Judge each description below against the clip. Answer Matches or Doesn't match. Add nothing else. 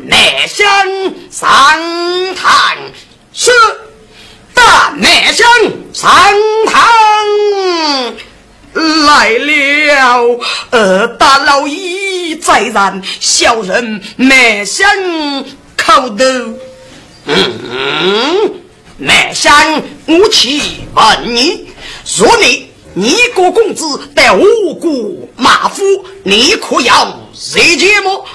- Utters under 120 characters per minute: Matches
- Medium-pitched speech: Doesn't match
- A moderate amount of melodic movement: Doesn't match